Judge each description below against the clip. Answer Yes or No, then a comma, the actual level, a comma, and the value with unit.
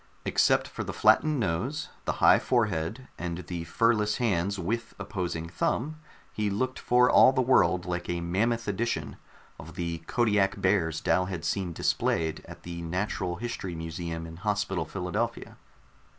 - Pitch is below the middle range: Yes, very low, 95 Hz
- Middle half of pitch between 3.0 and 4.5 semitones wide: No, average, 5.1 semitones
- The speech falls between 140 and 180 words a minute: Yes, average, 155 wpm